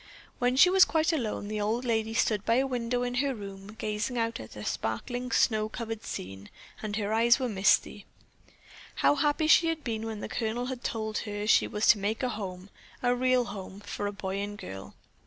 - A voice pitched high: Yes, high, 220 Hz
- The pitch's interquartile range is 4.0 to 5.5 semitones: No, average, 3.2 semitones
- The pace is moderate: No, fast, 210 wpm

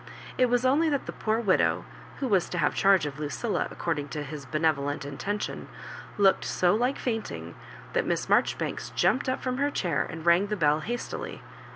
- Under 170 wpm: No, average, 185 wpm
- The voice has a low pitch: No, high, 195 Hz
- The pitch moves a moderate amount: No, wide, 7.9 semitones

